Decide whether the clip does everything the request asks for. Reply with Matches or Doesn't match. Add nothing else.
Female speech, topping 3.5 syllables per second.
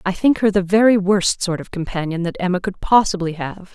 Matches